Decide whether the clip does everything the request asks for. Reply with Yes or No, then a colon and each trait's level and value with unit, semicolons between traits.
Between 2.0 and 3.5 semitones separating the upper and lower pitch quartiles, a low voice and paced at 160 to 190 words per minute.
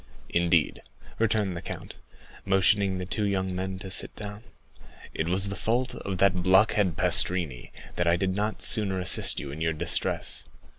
Yes: narrow, 2.4 semitones; very low, 95 Hz; average, 165 wpm